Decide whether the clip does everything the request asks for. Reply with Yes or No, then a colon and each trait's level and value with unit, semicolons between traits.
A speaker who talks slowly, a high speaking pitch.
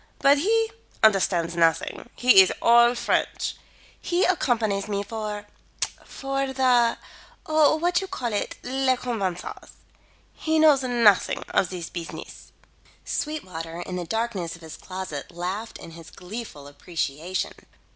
Yes: slow, 125 wpm; high, 215 Hz